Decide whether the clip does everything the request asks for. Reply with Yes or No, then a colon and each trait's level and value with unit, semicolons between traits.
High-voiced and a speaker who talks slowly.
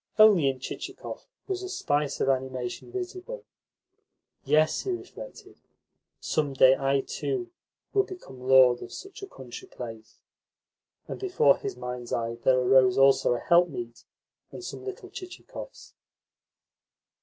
No: medium, 140 Hz; slow, 130 wpm